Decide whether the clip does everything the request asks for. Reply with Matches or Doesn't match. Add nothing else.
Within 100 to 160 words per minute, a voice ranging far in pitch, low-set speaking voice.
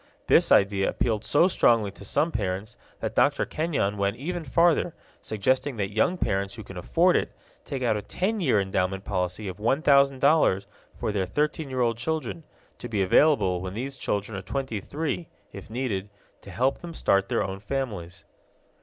Doesn't match